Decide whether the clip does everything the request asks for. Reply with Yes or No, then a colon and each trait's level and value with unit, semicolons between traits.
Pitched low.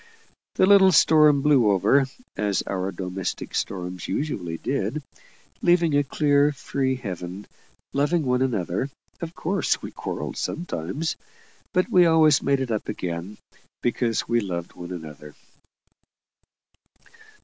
Yes: low, 130 Hz